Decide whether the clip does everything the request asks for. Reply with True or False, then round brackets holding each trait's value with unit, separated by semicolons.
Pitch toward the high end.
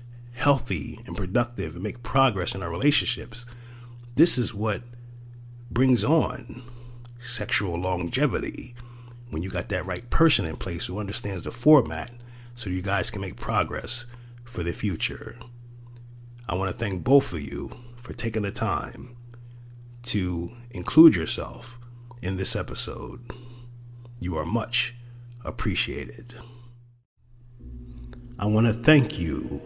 False (120 Hz)